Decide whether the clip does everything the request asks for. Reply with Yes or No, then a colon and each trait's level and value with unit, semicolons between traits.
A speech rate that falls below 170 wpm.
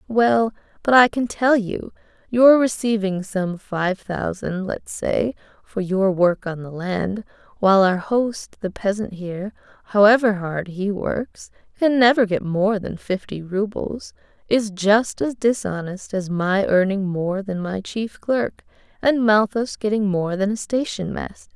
Yes: average, 155 wpm